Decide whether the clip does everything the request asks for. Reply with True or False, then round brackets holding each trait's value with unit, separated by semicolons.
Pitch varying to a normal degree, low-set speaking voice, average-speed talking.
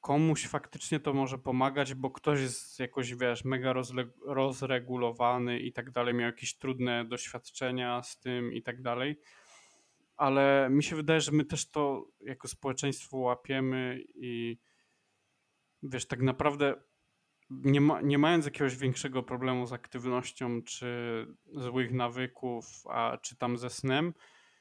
False (2.2 semitones; 130 Hz; 135 wpm)